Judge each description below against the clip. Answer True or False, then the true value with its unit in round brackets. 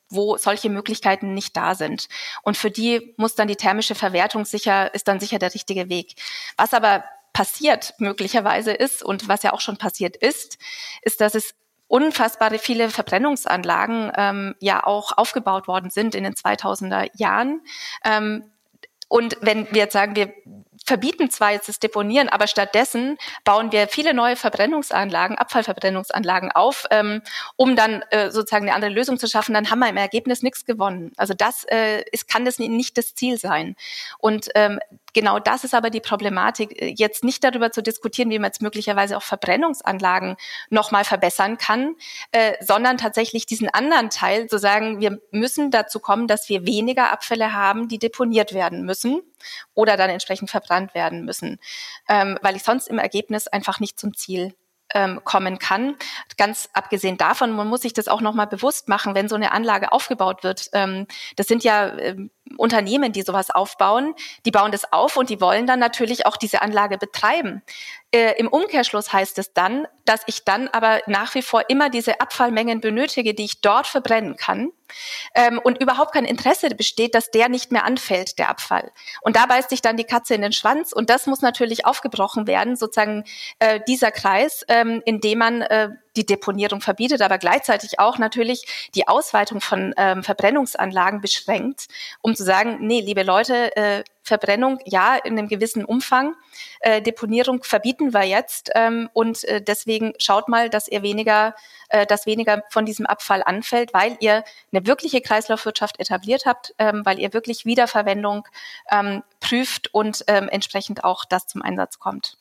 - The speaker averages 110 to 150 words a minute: False (175 wpm)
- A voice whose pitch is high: True (220 Hz)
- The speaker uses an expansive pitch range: False (3.1 semitones)